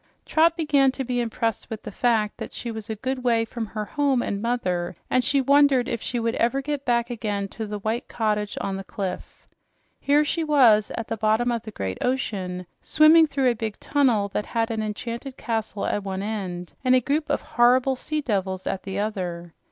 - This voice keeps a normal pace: No, fast, 210 wpm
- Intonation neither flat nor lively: Yes, average, 3.9 semitones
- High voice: Yes, high, 230 Hz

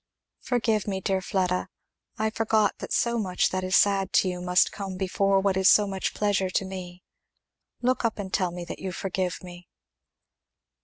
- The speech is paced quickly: No, average, 185 wpm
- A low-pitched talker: No, high, 190 Hz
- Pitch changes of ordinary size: No, narrow, 1.9 semitones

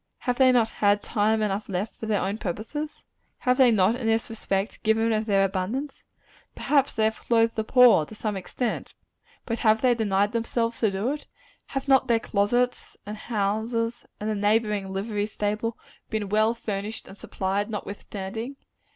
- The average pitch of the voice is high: Yes, high, 220 Hz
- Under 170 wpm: No, average, 175 wpm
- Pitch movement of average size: No, narrow, 2.3 semitones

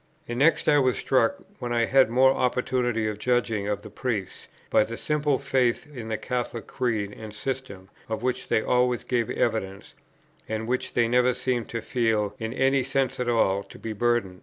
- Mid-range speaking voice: No, low, 120 Hz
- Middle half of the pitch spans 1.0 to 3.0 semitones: Yes, average, 2.7 semitones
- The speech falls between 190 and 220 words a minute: Yes, average, 195 wpm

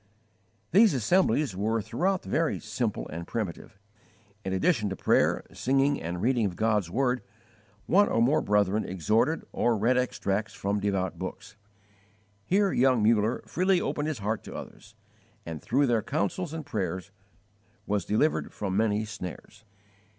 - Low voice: Yes, low, 110 Hz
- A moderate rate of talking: Yes, average, 145 wpm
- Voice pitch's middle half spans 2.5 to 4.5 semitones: No, wide, 5.4 semitones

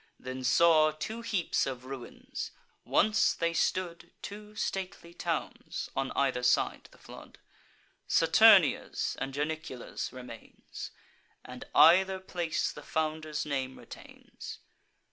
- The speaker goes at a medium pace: No, slow, 110 wpm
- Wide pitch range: Yes, wide, 5.9 semitones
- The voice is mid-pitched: Yes, medium, 155 Hz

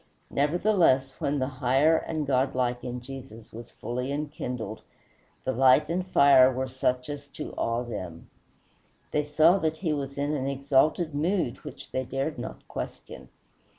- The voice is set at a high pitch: No, low, 135 Hz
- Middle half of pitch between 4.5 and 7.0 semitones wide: No, average, 2.9 semitones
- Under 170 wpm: Yes, average, 150 wpm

